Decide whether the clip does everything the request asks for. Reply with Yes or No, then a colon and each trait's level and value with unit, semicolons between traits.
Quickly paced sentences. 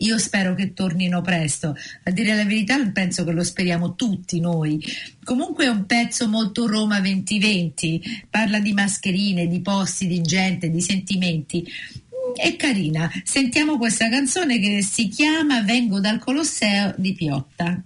No: average, 150 wpm